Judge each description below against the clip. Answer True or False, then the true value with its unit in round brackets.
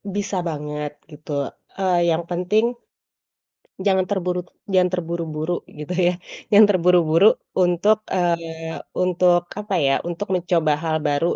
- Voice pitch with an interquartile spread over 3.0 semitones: False (2.5 semitones)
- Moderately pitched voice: True (175 Hz)